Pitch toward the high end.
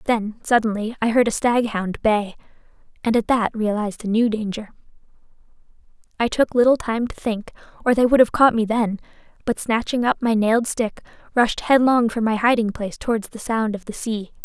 Yes: high, 225 Hz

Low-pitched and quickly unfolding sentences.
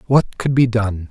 Yes: low, 115 Hz; fast, 220 wpm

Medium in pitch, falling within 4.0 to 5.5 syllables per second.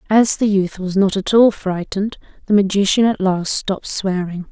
No: high, 195 Hz; 5.0 syllables/s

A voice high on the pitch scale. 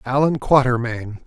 No: low, 125 Hz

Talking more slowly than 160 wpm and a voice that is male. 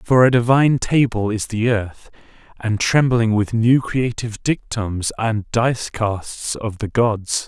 Yes: average, 150 wpm; male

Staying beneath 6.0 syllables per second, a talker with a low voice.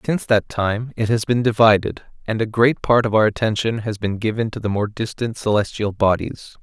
Yes: 5.4 syllables/s; low, 110 Hz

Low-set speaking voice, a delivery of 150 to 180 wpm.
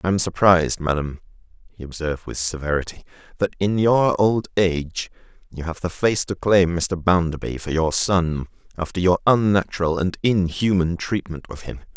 Yes: very low, 90 Hz; average, 160 wpm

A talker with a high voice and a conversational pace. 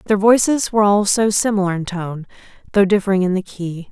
Yes: high, 195 Hz; average, 185 wpm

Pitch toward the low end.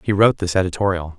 Yes: very low, 95 Hz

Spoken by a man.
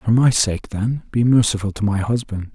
Yes: male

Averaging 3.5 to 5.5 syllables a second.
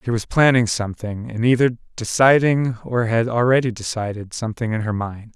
Yes: 5.2 syllables/s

